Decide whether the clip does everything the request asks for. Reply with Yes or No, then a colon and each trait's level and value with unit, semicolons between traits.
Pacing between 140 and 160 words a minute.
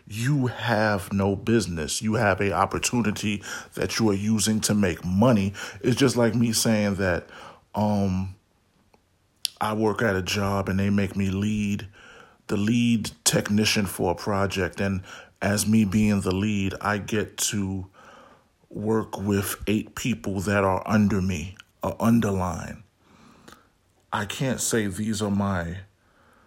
Yes: average, 145 wpm